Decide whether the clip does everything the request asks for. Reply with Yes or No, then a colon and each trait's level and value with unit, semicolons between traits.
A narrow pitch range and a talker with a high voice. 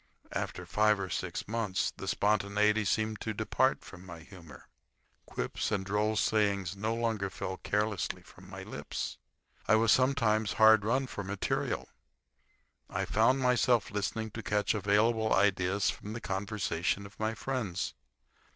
No: narrow, 2.0 semitones; low, 105 Hz